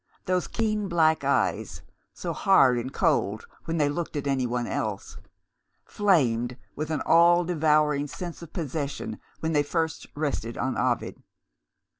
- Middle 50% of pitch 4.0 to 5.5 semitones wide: Yes, average, 4.4 semitones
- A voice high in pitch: No, medium, 155 Hz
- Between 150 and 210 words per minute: No, average, 140 wpm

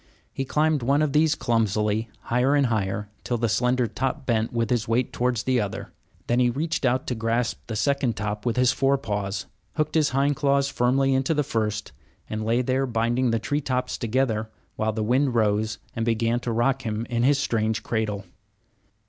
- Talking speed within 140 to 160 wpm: No, average, 195 wpm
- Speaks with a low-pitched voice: Yes, low, 120 Hz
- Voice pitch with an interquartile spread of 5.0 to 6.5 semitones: No, average, 3.4 semitones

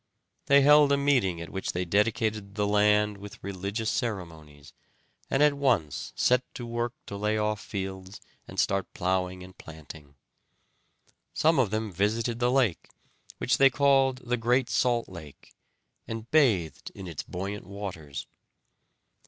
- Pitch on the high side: No, low, 105 Hz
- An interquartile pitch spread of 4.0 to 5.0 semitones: Yes, average, 4.7 semitones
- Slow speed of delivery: No, average, 145 wpm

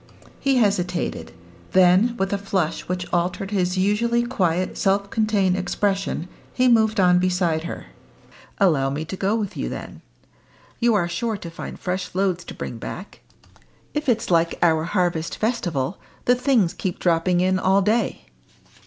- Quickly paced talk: No, average, 155 wpm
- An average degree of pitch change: Yes, average, 3.2 semitones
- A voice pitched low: No, medium, 185 Hz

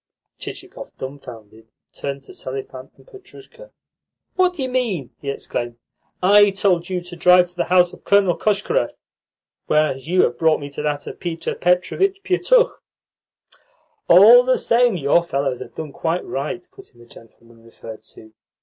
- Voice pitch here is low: No, medium, 175 Hz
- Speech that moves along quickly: No, average, 160 wpm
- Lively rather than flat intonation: Yes, wide, 7.3 semitones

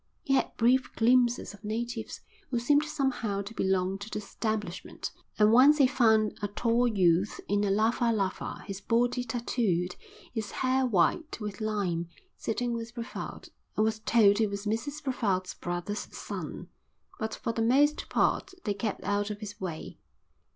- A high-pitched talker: Yes, high, 220 Hz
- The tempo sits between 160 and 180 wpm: Yes, average, 165 wpm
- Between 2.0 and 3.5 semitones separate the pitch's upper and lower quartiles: Yes, average, 3.1 semitones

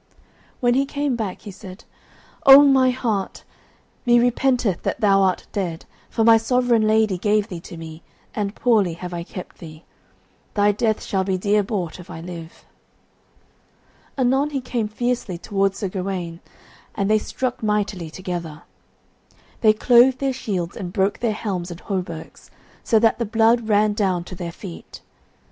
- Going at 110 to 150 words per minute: No, average, 165 wpm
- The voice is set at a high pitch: Yes, high, 205 Hz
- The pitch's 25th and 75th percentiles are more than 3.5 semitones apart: Yes, average, 4.5 semitones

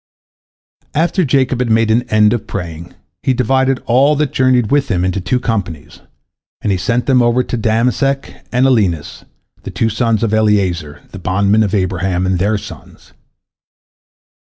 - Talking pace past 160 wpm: No, average, 155 wpm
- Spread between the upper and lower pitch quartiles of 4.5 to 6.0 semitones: Yes, average, 4.8 semitones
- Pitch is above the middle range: No, low, 110 Hz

